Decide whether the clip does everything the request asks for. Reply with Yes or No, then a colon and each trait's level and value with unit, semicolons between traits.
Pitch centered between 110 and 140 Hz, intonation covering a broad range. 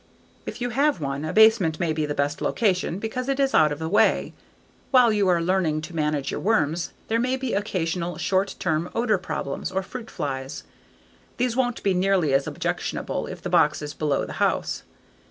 No: medium, 185 Hz; wide, 6.4 semitones